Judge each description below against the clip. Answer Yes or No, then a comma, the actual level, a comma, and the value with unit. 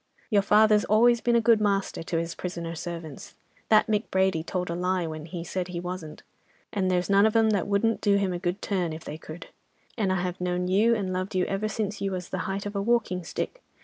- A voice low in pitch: No, high, 190 Hz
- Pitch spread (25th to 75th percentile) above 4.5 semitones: No, average, 2.9 semitones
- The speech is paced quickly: Yes, fast, 240 wpm